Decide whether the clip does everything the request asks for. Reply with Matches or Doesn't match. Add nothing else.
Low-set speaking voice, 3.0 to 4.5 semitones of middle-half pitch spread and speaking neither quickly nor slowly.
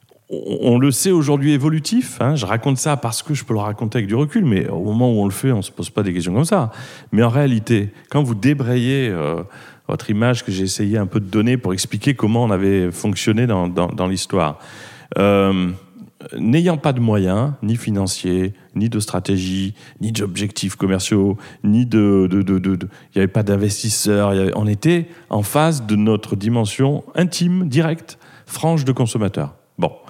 Doesn't match